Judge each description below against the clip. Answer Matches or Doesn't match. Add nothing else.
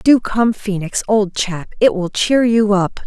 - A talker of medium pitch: Doesn't match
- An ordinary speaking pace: Matches